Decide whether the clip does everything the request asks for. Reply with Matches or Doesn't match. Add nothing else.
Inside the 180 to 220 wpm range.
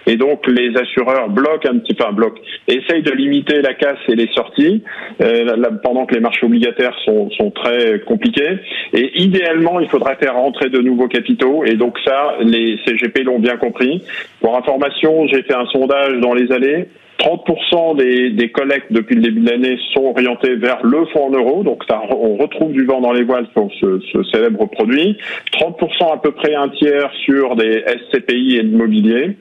Matches